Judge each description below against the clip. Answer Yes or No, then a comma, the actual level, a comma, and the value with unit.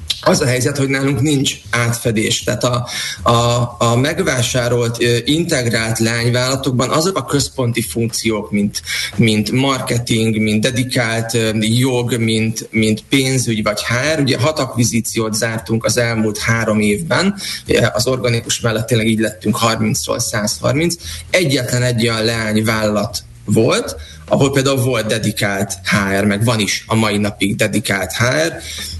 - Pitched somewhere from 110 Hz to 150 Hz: Yes, low, 115 Hz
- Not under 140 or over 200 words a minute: No, average, 130 wpm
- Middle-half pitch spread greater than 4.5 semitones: No, average, 2.7 semitones